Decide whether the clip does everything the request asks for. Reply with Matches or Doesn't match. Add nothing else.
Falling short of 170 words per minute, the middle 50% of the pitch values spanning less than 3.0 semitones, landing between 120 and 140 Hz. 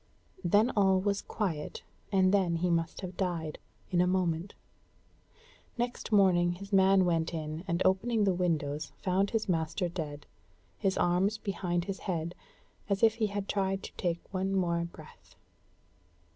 Doesn't match